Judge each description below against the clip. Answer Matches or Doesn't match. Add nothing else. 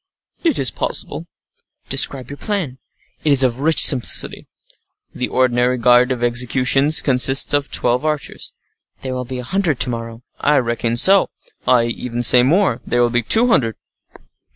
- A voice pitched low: Matches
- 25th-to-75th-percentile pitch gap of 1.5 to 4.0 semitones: Matches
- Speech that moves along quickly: Doesn't match